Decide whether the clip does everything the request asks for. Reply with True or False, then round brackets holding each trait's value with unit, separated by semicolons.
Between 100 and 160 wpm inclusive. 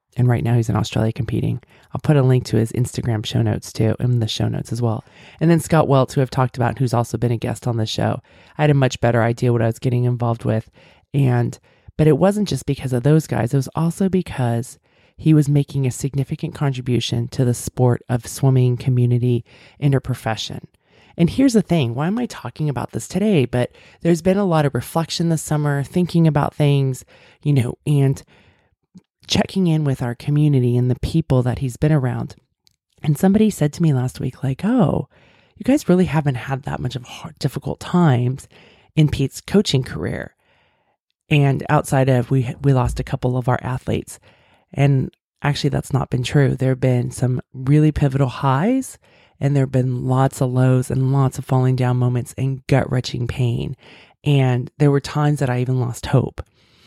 False (200 wpm)